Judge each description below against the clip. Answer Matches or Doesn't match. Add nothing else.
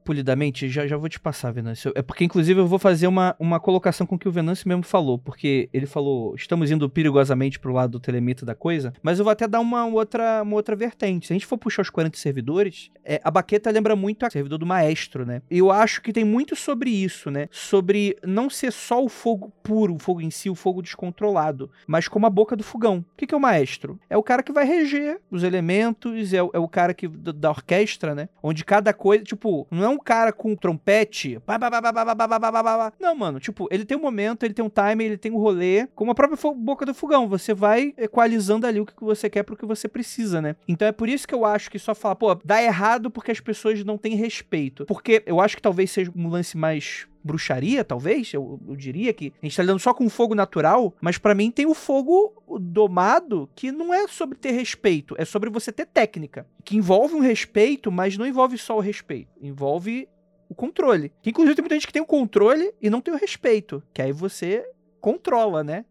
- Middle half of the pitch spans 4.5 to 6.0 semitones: Matches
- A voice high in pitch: Matches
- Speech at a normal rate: Doesn't match